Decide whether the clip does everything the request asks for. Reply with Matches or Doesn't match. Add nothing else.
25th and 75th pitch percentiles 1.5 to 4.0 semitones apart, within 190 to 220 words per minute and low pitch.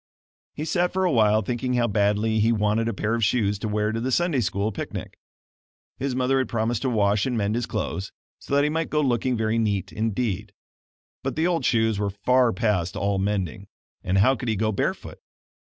Matches